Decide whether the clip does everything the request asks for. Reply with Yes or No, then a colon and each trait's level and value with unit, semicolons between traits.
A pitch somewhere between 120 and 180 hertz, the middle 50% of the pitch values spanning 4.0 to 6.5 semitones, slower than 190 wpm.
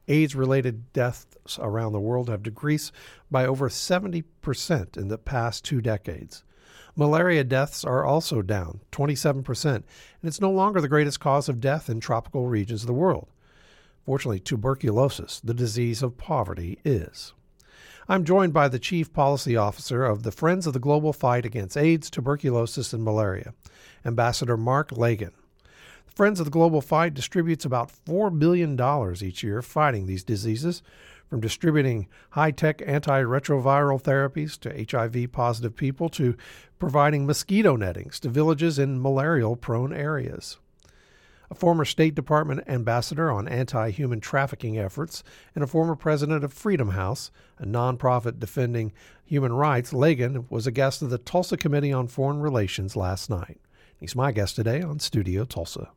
Yes: low, 135 Hz; average, 4.6 semitones; average, 150 wpm